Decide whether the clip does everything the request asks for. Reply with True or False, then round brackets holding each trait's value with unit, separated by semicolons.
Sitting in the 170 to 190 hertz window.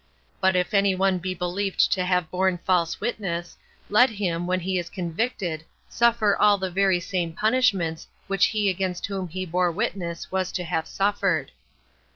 True (185 Hz)